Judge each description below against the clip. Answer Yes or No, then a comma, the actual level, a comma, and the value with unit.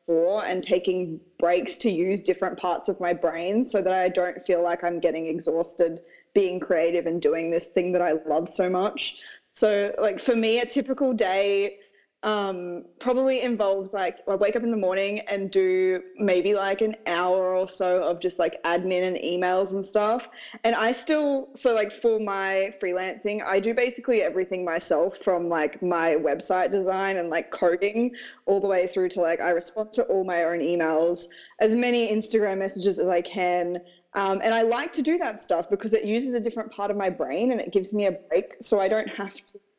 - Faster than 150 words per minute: Yes, average, 200 wpm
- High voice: Yes, high, 195 Hz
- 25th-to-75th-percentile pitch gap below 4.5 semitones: Yes, average, 3.7 semitones